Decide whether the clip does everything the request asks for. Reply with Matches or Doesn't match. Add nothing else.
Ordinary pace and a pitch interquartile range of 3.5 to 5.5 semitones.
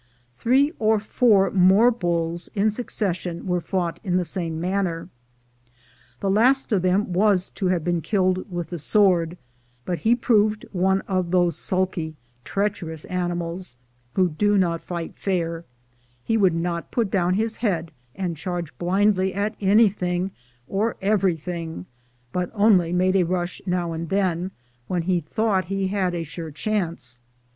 Doesn't match